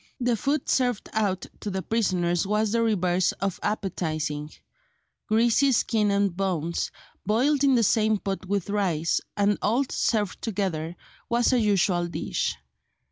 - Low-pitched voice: No, high, 205 Hz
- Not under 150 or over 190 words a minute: No, average, 140 wpm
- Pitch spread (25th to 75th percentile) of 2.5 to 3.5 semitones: No, average, 3.9 semitones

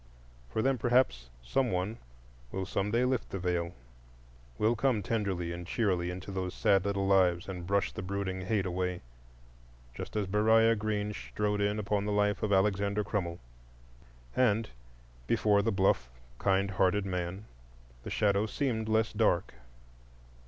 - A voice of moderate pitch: No, low, 100 Hz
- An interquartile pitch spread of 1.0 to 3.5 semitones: Yes, average, 2.8 semitones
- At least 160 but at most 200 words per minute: No, average, 145 wpm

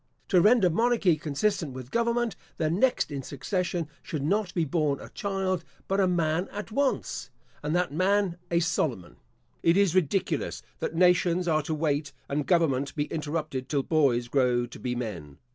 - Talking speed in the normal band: Yes, average, 170 wpm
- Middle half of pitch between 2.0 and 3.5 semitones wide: No, average, 4.7 semitones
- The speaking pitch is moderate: Yes, medium, 165 Hz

